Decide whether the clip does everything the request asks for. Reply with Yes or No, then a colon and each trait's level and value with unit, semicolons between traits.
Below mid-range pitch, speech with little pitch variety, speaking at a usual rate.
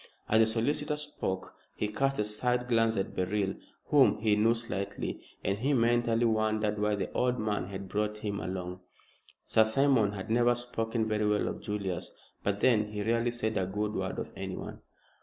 Yes: low, 110 Hz; narrow, 2.3 semitones; average, 180 wpm